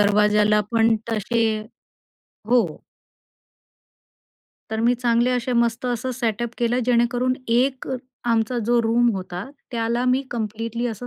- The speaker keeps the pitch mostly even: Yes, narrow, 1.6 semitones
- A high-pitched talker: Yes, high, 235 Hz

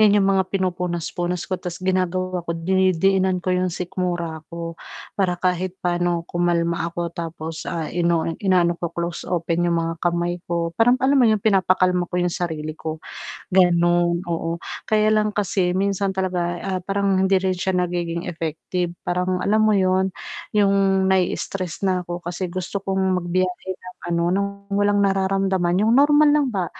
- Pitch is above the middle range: No, medium, 180 Hz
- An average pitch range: No, narrow, 1.9 semitones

